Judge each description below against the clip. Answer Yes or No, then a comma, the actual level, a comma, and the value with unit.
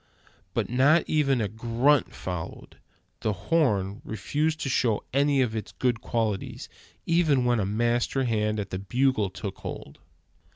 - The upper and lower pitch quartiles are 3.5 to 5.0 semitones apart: Yes, average, 4.5 semitones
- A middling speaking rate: Yes, average, 150 wpm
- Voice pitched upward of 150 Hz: No, low, 120 Hz